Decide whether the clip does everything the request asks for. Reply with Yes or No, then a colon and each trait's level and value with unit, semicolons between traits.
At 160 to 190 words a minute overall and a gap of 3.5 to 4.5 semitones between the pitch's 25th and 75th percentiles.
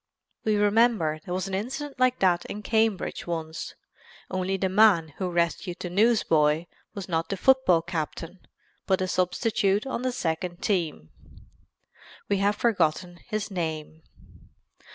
No: average, 140 wpm; average, 3.9 semitones